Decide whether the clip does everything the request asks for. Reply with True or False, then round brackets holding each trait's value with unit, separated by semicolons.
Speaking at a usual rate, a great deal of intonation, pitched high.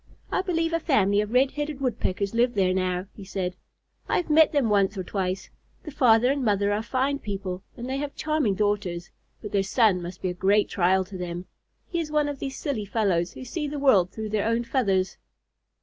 False (215 wpm; 6.3 semitones; 210 Hz)